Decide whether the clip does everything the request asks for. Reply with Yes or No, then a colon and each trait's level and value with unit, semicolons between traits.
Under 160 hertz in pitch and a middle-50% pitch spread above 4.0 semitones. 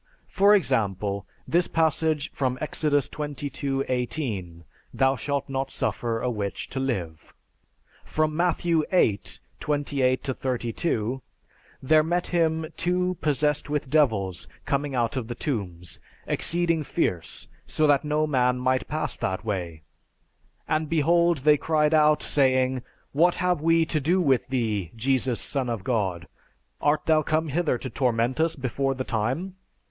Yes: medium, 140 Hz; average, 4.5 semitones